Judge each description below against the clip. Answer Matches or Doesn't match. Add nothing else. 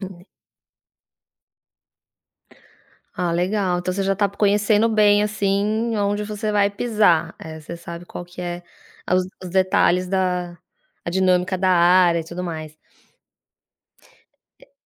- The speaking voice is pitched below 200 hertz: Matches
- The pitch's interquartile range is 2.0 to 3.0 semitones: Matches